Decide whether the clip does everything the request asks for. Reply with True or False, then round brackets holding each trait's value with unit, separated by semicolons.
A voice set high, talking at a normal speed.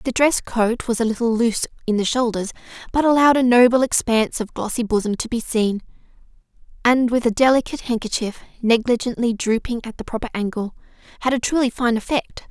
True (235 Hz; 175 wpm)